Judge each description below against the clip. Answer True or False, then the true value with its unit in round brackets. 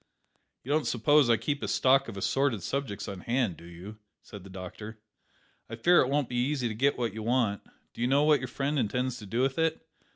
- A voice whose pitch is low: True (125 Hz)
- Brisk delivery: True (230 wpm)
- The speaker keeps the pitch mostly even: False (4.5 semitones)